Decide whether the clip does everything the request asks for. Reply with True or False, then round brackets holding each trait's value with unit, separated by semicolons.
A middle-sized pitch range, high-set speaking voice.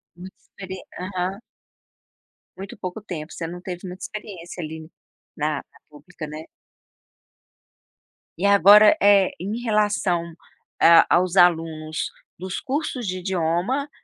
False (3.2 semitones; 180 Hz)